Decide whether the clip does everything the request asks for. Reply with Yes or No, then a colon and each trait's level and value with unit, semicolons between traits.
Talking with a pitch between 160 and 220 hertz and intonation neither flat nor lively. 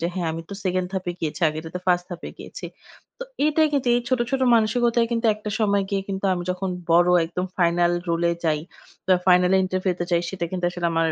Yes: medium, 185 Hz; average, 3.4 semitones